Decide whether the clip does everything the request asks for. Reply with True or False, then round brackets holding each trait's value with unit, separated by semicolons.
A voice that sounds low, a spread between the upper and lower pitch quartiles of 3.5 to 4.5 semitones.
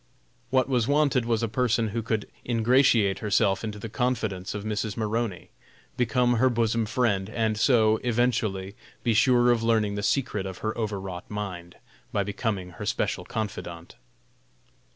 False (110 Hz; 2.9 semitones)